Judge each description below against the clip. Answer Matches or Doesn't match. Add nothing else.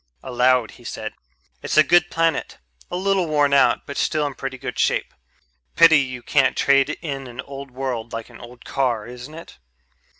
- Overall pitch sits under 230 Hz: Matches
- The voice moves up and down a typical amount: Matches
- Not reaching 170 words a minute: Doesn't match